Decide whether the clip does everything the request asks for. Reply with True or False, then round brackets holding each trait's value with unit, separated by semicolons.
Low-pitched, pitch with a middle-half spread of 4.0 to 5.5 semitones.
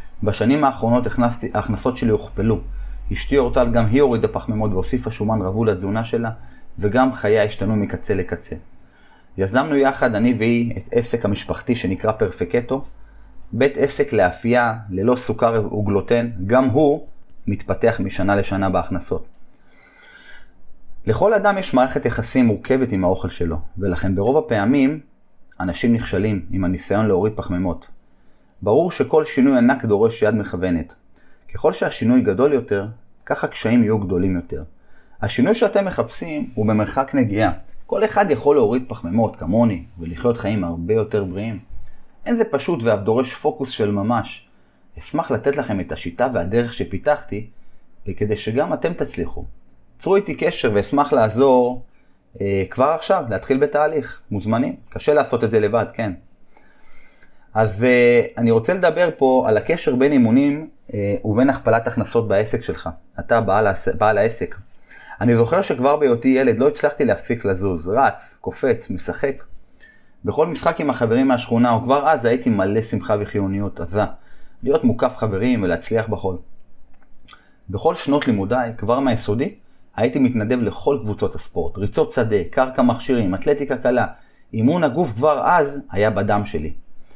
True (115 Hz; 4.5 semitones)